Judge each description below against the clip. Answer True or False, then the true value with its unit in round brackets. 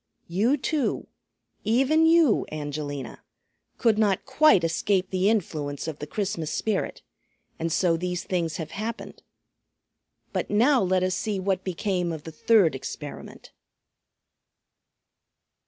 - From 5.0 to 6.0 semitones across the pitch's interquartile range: True (5.3 semitones)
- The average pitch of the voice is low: False (185 Hz)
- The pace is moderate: False (120 wpm)